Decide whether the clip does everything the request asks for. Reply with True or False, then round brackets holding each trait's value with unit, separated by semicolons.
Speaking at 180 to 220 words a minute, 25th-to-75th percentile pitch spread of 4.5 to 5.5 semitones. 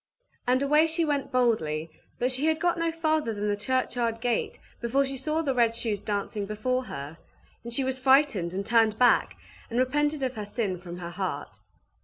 True (195 wpm; 4.9 semitones)